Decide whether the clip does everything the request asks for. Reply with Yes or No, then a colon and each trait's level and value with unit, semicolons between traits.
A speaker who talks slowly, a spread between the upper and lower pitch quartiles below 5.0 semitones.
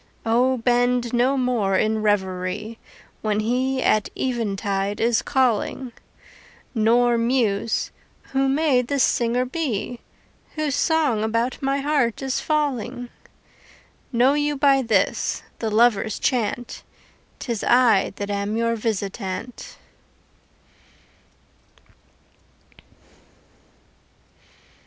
Yes: slow, 95 wpm; average, 3.4 semitones